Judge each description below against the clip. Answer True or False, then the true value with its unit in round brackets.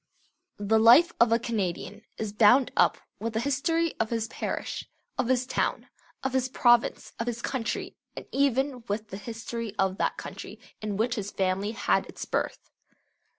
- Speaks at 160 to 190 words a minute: True (170 wpm)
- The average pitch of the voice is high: True (230 Hz)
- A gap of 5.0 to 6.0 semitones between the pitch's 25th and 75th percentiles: False (3.3 semitones)